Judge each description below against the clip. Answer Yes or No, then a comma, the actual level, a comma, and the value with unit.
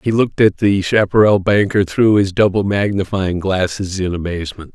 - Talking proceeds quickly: No, average, 165 wpm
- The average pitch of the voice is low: Yes, low, 100 Hz